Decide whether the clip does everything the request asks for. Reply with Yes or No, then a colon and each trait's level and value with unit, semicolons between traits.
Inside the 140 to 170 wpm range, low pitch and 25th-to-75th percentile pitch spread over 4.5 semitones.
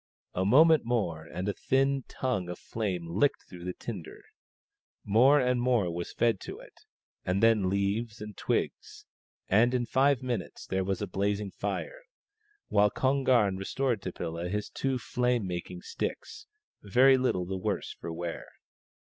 Yes: average, 160 wpm; low, 105 Hz; wide, 5.4 semitones